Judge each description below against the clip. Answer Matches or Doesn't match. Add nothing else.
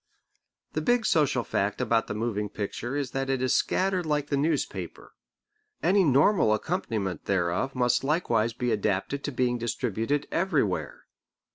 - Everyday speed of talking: Matches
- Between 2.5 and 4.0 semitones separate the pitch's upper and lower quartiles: Doesn't match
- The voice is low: Matches